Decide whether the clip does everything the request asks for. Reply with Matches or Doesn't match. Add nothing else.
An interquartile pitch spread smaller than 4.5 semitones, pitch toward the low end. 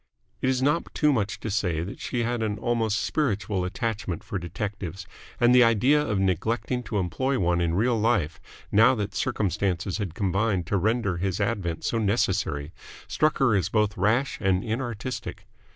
Matches